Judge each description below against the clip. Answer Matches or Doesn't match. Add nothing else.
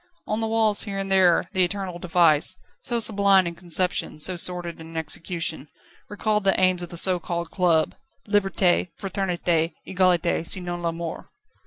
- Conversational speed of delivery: Matches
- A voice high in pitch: Doesn't match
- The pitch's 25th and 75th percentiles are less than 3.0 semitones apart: Matches